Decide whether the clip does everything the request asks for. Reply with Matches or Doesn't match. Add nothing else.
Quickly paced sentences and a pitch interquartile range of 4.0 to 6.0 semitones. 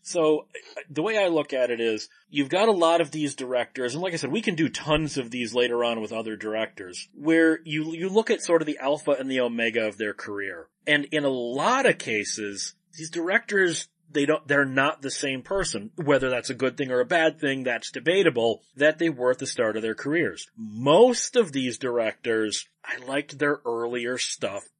Matches